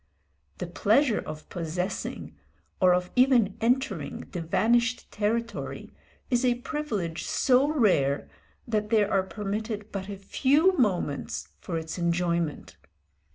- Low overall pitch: No, high, 210 Hz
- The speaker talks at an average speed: No, slow, 120 wpm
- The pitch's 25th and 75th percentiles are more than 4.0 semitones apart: Yes, average, 5.2 semitones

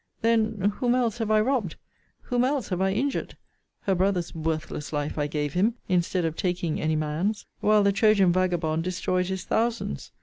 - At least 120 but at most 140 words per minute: No, average, 175 wpm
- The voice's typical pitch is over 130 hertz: Yes, medium, 185 Hz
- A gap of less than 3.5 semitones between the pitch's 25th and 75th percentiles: No, average, 4.9 semitones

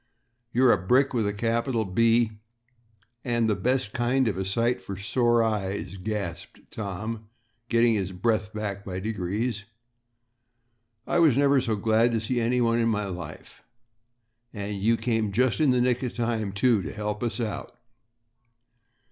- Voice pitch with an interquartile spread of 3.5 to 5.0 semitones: No, average, 2.9 semitones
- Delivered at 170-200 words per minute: No, average, 155 wpm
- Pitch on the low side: Yes, low, 110 Hz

